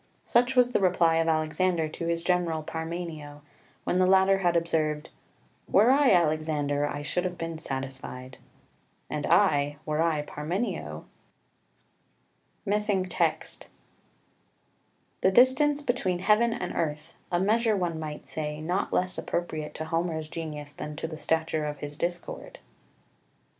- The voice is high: No, medium, 165 Hz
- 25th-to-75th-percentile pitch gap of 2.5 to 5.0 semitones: Yes, average, 3.5 semitones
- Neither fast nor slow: No, slow, 130 wpm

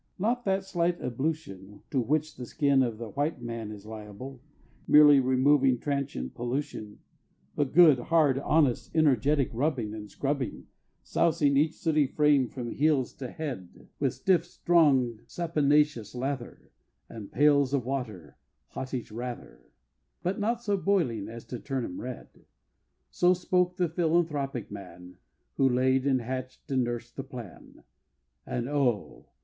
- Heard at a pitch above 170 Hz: No, low, 135 Hz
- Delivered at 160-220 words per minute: No, average, 140 wpm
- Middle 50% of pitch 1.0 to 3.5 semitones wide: No, average, 4.3 semitones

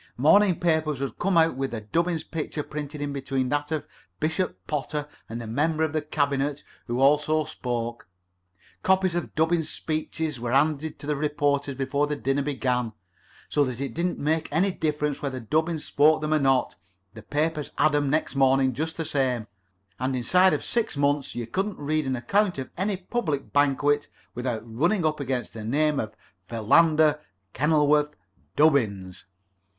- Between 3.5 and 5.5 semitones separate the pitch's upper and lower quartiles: No, average, 2.9 semitones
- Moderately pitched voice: Yes, medium, 145 Hz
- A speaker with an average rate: Yes, average, 165 wpm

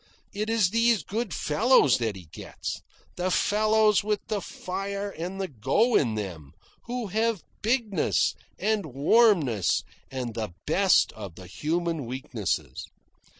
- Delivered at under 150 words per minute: Yes, slow, 135 wpm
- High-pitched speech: No, medium, 180 Hz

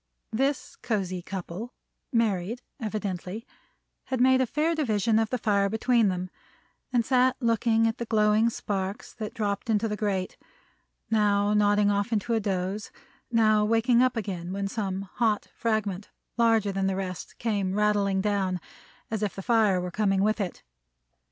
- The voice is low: No, high, 210 Hz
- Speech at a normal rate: Yes, average, 160 wpm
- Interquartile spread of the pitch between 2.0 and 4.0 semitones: Yes, narrow, 2.6 semitones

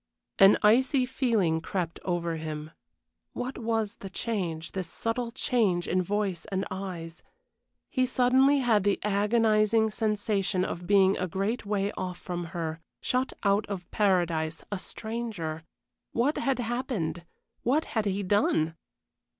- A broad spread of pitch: No, average, 4.6 semitones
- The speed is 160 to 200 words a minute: No, slow, 135 wpm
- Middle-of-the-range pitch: No, high, 200 Hz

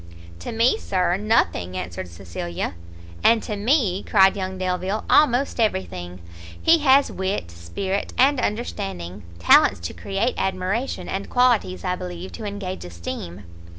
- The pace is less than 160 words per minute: Yes, average, 140 wpm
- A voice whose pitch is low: No, high, 190 Hz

